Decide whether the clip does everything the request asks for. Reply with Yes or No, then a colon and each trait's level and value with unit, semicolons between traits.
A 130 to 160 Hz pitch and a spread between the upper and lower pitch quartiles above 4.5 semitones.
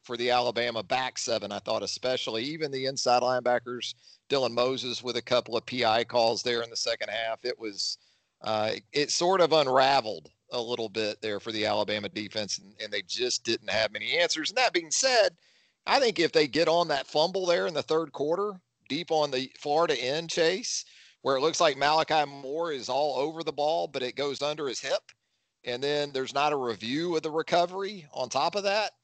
Yes: low, 135 Hz; average, 5.3 semitones